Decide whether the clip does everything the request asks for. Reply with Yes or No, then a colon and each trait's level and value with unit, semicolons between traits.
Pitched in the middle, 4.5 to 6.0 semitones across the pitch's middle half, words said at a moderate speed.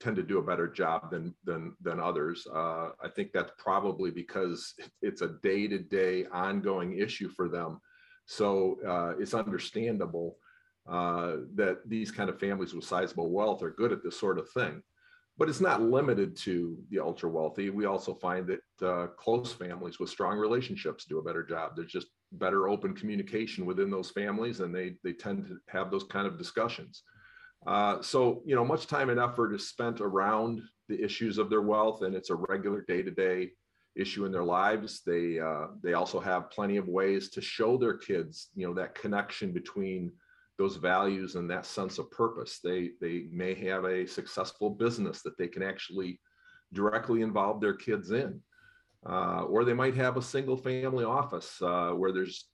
No: low, 100 Hz; wide, 5.5 semitones; average, 185 wpm